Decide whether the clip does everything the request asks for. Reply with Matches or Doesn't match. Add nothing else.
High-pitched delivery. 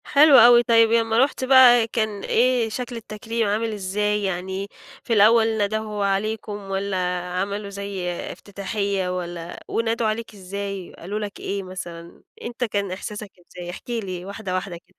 Matches